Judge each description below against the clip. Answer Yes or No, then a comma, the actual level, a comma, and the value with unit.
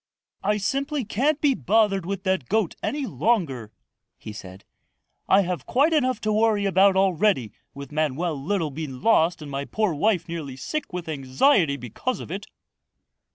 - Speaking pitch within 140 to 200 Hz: Yes, high, 190 Hz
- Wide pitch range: Yes, wide, 6.8 semitones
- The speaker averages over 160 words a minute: No, average, 155 wpm